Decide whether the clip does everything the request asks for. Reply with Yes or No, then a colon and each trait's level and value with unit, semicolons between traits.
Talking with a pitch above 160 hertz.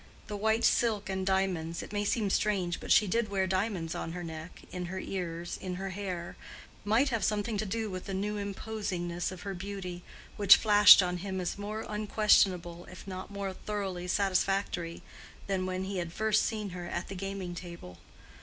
Yes: high, 190 Hz